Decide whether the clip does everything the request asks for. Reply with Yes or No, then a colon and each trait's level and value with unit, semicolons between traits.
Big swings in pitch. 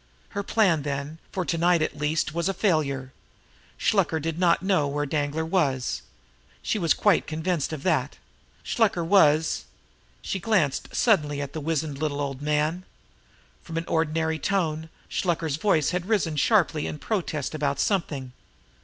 No: average, 3.4 semitones